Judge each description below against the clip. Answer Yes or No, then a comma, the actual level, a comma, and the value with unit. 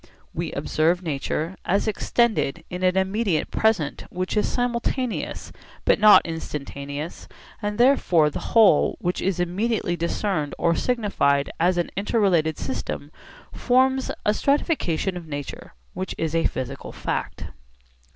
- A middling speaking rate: No, slow, 130 wpm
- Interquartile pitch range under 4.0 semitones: No, wide, 5.4 semitones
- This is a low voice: No, medium, 180 Hz